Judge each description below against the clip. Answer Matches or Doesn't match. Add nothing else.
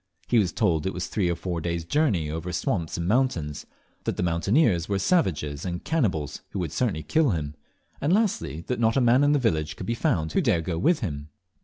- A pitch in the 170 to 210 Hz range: Doesn't match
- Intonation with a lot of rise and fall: Matches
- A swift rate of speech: Matches